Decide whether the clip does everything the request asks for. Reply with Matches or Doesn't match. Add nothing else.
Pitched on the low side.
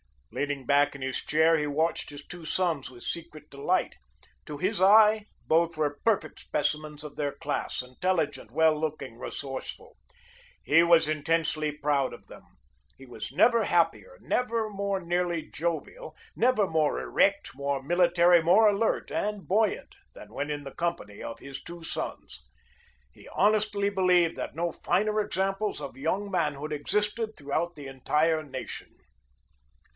Doesn't match